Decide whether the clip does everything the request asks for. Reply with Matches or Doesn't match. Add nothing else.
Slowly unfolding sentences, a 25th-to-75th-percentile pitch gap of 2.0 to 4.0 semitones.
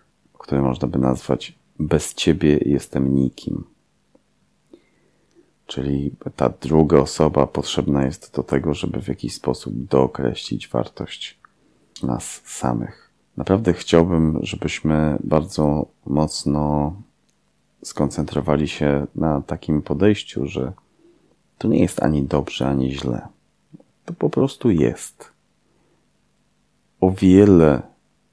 Matches